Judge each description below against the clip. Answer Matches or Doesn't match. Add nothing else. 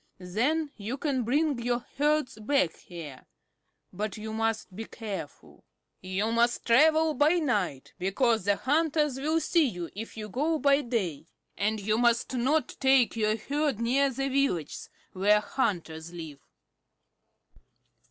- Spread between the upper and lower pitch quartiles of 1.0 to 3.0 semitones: Doesn't match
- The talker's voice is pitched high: Matches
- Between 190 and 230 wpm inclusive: Doesn't match